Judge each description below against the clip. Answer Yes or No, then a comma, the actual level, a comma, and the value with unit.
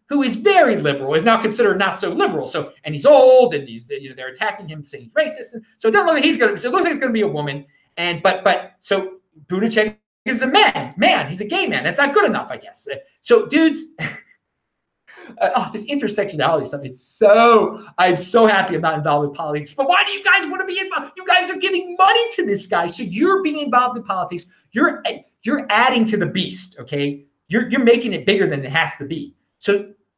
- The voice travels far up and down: Yes, wide, 8.7 semitones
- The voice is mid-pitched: No, high, 215 Hz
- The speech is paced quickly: Yes, fast, 240 wpm